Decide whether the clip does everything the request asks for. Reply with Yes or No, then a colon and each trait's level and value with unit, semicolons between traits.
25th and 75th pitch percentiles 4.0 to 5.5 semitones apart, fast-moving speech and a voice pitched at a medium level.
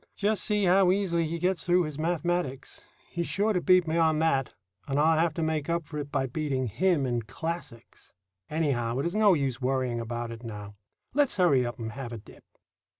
Yes: average, 5.2 semitones; fast, 210 wpm; medium, 155 Hz